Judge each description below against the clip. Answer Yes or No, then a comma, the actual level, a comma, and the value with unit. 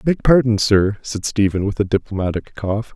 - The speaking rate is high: No, average, 185 wpm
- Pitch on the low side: Yes, low, 105 Hz